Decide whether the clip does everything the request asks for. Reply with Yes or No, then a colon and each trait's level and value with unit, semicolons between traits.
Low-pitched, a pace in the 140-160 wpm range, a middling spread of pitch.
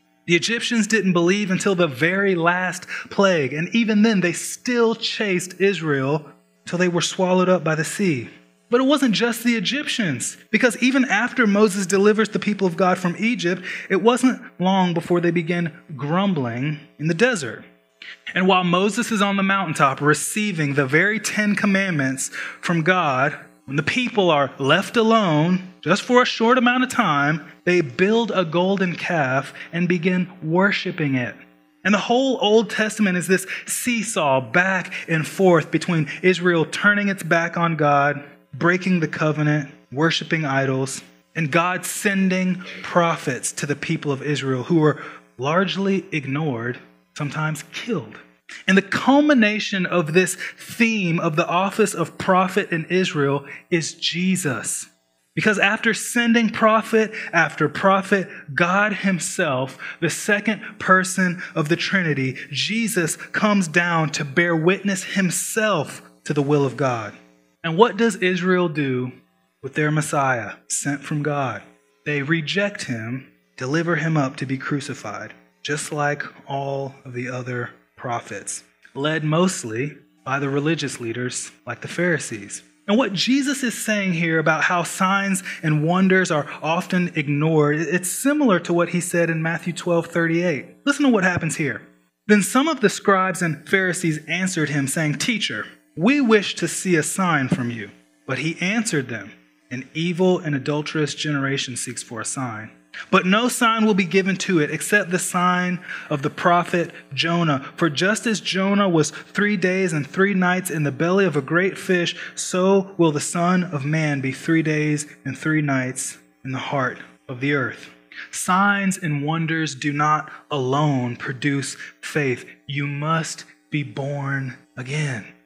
No: medium, 170 Hz; average, 155 wpm; average, 5.0 semitones